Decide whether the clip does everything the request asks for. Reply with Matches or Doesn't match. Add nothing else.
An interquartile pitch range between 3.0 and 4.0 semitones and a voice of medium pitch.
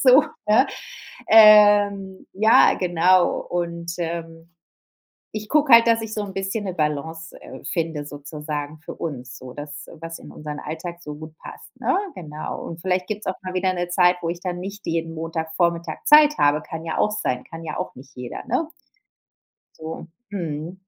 Matches